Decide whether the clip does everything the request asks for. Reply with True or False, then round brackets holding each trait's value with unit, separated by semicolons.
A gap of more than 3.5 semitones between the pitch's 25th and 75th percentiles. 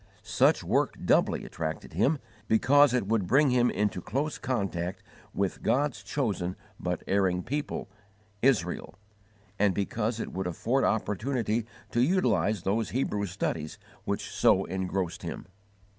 True (5.2 semitones)